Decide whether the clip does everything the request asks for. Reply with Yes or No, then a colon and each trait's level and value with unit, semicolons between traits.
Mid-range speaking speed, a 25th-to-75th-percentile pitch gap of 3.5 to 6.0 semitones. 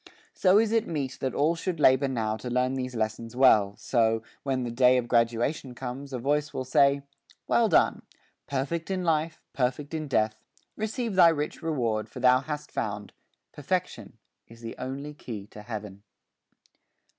Yes: average, 170 wpm; average, 4.3 semitones